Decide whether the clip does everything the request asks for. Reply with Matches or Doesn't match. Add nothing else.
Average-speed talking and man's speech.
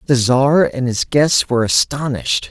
Matches